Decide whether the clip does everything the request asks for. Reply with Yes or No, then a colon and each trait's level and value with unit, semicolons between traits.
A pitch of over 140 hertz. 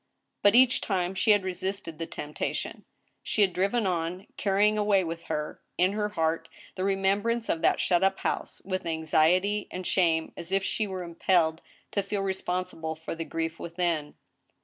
Yes: medium, 185 Hz